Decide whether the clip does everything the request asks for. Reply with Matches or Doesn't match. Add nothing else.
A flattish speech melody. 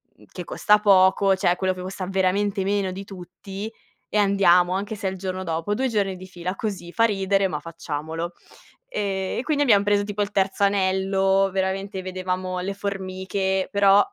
Matches